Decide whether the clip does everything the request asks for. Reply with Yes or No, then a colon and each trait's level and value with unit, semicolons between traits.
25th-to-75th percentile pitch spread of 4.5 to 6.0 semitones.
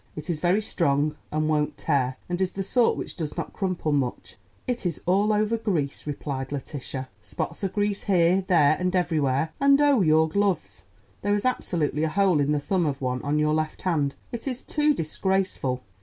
Yes: average, 5.3 semitones